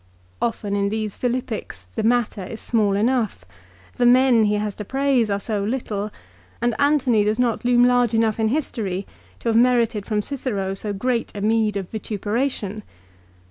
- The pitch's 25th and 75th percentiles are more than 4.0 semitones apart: No, average, 2.9 semitones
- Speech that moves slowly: No, average, 170 wpm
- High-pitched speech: Yes, high, 220 Hz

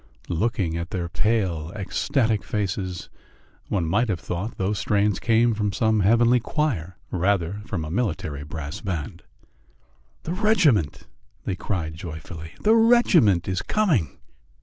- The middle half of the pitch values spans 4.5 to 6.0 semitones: Yes, average, 5.2 semitones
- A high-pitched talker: No, low, 100 Hz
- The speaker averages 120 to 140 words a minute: Yes, slow, 135 wpm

